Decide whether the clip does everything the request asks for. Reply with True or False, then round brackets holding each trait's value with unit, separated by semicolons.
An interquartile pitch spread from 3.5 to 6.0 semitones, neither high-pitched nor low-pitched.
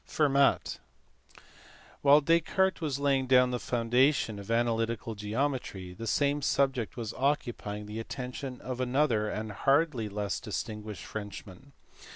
False (4.5 semitones; 125 Hz)